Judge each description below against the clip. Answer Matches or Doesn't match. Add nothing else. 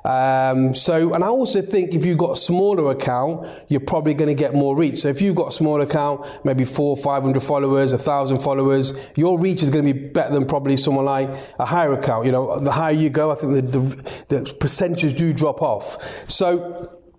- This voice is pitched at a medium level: Matches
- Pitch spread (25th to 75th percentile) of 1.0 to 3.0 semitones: Doesn't match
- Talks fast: Matches